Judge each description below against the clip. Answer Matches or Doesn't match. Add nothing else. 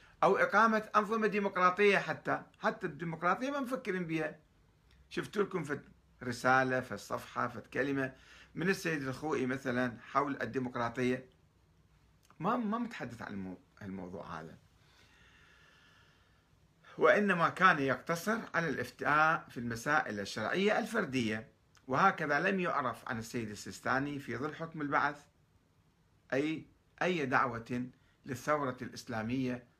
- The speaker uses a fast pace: Doesn't match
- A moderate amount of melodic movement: Doesn't match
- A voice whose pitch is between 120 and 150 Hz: Matches